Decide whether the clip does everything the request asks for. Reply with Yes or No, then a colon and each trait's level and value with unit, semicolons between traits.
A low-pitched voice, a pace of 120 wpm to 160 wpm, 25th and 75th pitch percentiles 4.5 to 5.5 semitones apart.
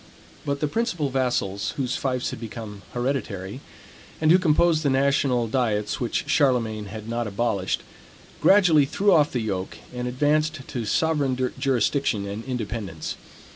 Yes: low, 125 Hz; average, 140 wpm; average, 4.9 semitones